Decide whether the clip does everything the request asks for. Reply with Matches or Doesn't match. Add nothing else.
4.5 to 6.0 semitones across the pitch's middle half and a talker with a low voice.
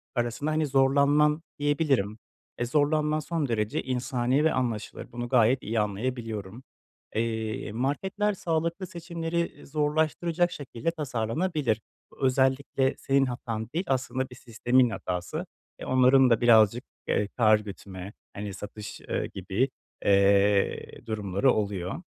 Matches